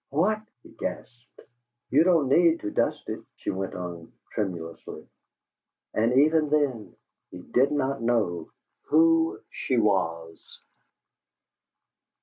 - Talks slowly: Yes, slow, 115 wpm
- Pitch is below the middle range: Yes, low, 125 Hz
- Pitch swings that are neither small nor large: No, wide, 8.5 semitones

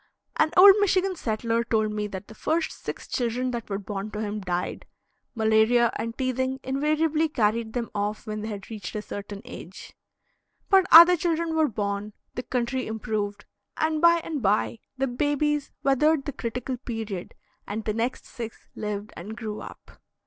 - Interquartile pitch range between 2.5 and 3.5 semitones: No, wide, 5.4 semitones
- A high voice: Yes, high, 230 Hz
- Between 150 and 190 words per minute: Yes, average, 170 wpm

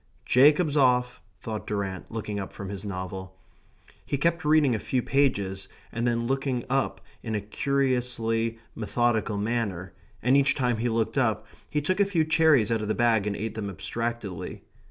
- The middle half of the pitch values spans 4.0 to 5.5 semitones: Yes, average, 4.5 semitones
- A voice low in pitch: Yes, low, 115 Hz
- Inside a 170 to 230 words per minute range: Yes, average, 175 wpm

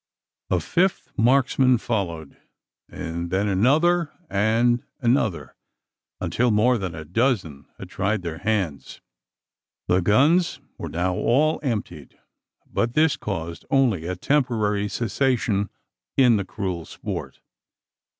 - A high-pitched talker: No, low, 110 Hz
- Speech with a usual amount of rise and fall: No, wide, 5.9 semitones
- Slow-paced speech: Yes, slow, 115 wpm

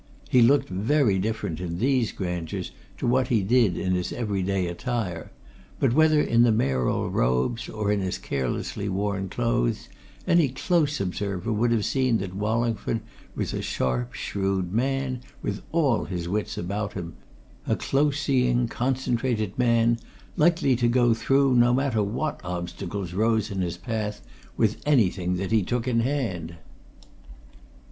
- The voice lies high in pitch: No, low, 110 Hz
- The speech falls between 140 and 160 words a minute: Yes, average, 150 wpm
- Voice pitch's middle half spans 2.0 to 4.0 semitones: No, average, 5.0 semitones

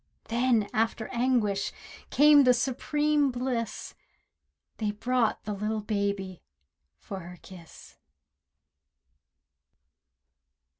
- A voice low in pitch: No, high, 225 Hz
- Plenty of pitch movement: No, average, 4.0 semitones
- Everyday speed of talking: No, slow, 85 wpm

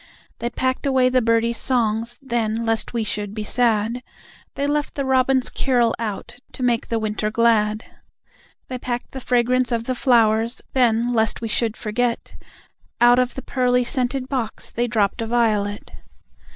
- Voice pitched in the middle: No, high, 235 Hz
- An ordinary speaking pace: Yes, average, 165 wpm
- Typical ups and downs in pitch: No, narrow, 2.2 semitones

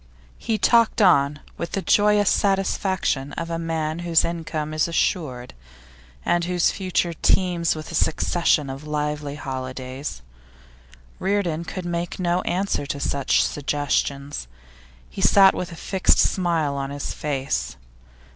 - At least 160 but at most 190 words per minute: No, slow, 135 wpm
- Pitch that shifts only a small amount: No, average, 4.2 semitones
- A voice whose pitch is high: No, medium, 165 Hz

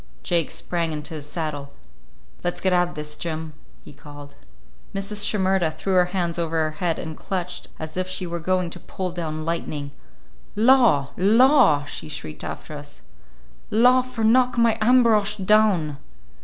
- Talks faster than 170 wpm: No, average, 160 wpm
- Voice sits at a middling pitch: Yes, medium, 175 Hz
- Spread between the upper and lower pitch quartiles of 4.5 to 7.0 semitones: Yes, average, 5.0 semitones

